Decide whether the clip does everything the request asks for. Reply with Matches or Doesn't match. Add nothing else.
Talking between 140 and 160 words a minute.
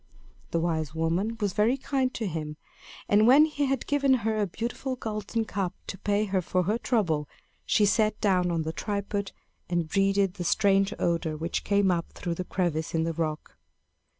Doesn't match